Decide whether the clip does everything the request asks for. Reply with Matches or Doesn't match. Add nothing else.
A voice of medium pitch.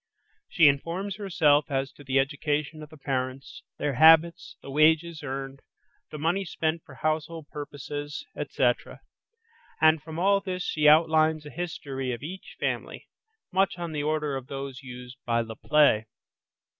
Matches